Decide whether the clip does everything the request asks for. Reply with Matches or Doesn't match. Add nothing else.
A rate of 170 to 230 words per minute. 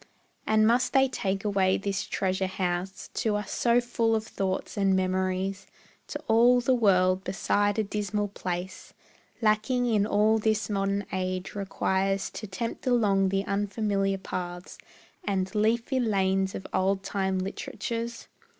Doesn't match